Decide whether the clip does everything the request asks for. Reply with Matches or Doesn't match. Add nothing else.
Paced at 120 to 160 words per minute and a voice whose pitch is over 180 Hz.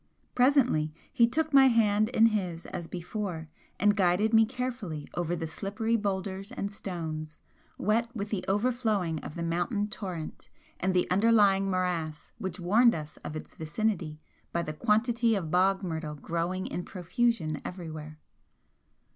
Matches